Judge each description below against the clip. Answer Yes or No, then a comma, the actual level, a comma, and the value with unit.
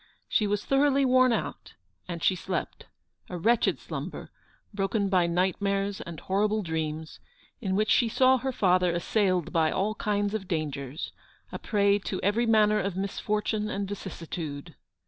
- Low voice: No, high, 200 Hz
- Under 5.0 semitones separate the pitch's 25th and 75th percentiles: Yes, average, 3.2 semitones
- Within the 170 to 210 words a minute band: No, average, 150 wpm